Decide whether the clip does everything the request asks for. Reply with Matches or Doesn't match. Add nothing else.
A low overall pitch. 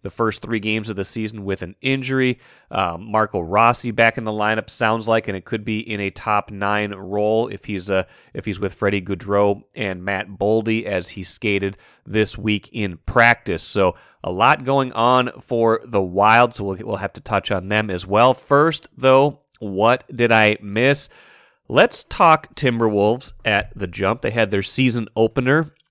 Matches